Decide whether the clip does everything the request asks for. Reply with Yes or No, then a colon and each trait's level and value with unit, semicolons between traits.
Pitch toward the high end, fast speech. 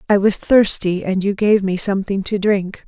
Yes: high, 195 Hz; fast, 210 wpm